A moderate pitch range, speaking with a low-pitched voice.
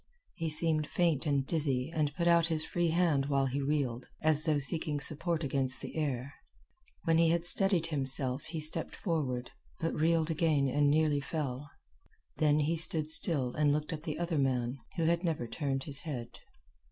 No: average, 3.0 semitones; medium, 150 Hz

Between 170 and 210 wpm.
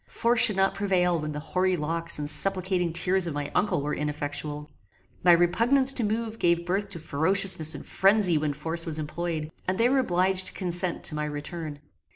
Yes: average, 195 wpm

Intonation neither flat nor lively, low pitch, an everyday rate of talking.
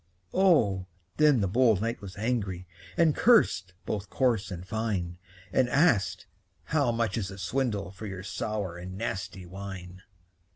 Yes: average, 4.3 semitones; low, 100 Hz; average, 150 wpm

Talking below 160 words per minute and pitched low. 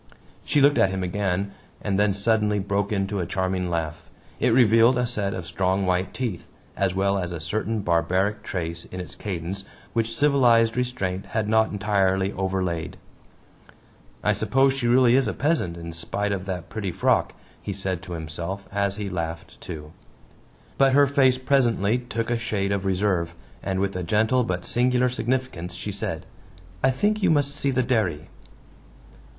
No: average, 170 wpm; low, 100 Hz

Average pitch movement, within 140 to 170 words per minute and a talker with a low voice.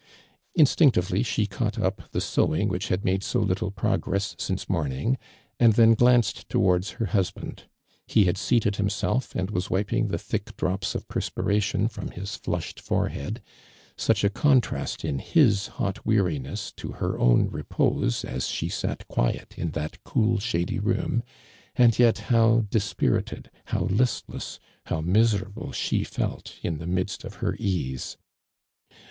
Yes: average, 4.0 semitones; average, 150 wpm; low, 100 Hz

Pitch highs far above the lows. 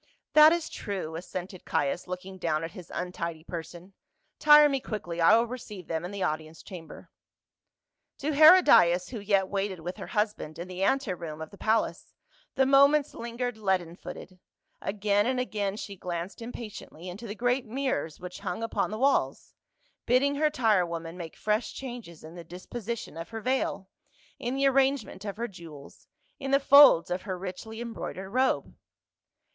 Yes: wide, 5.7 semitones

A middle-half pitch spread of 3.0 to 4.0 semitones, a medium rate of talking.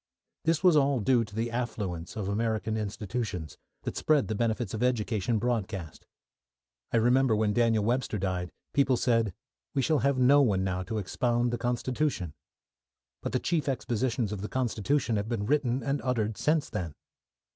Yes: average, 3.6 semitones; average, 170 wpm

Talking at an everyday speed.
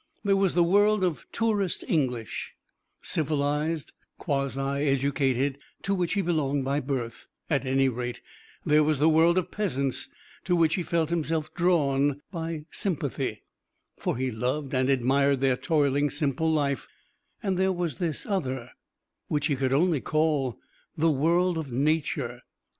Yes: average, 145 wpm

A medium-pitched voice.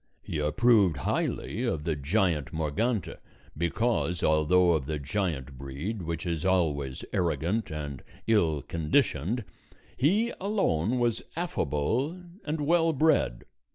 No: very low, 85 Hz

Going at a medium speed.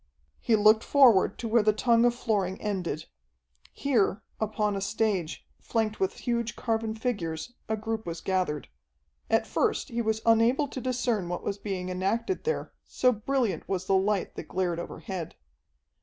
Yes: average, 160 wpm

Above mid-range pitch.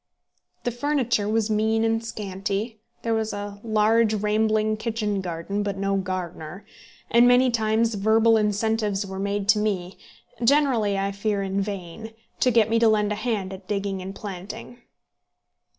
Yes: high, 210 Hz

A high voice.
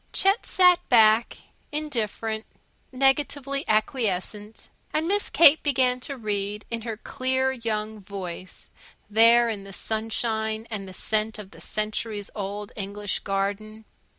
Yes: high, 220 Hz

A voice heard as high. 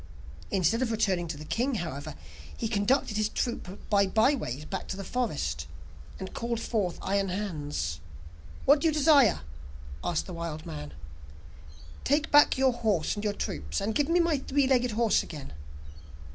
Yes: high, 210 Hz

